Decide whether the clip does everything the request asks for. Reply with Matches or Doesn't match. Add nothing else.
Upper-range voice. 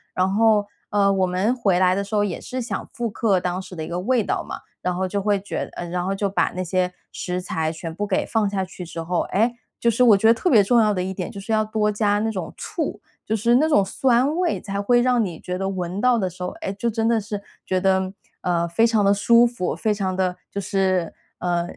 Matches